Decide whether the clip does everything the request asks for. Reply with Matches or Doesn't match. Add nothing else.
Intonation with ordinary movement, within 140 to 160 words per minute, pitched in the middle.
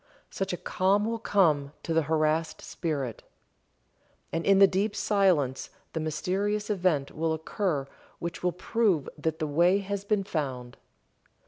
Matches